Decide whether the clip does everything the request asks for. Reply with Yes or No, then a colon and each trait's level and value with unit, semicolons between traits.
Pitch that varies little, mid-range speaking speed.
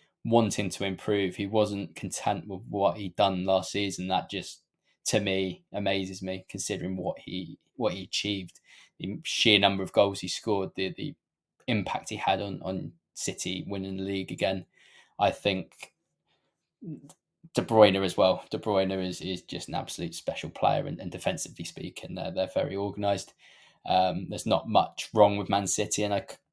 Yes: narrow, 1.4 semitones; average, 170 wpm